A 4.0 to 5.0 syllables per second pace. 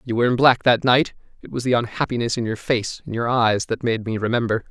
No: 6.1 syllables/s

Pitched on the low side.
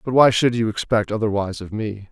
Yes: low, 110 Hz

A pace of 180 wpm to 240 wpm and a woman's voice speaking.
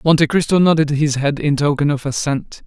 No: average, 200 wpm; male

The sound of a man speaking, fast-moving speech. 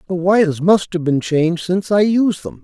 Yes: male; fast, 225 wpm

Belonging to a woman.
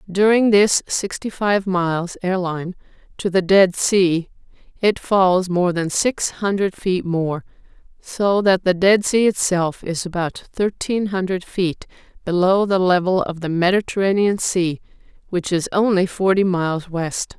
Yes: female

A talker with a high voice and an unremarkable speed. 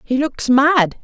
Yes: very high, 270 Hz; average, 175 wpm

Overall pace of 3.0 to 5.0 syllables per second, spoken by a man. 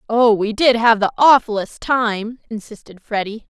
No: 4.5 syllables/s; female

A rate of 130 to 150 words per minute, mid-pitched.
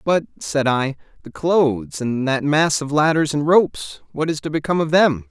No: fast, 205 wpm; medium, 145 Hz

